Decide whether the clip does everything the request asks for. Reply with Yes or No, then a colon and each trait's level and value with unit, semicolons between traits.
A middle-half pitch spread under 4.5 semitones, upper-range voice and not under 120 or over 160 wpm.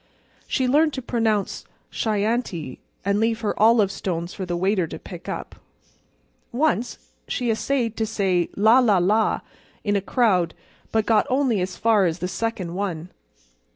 Yes: average, 3.8 semitones; high, 215 Hz; average, 155 wpm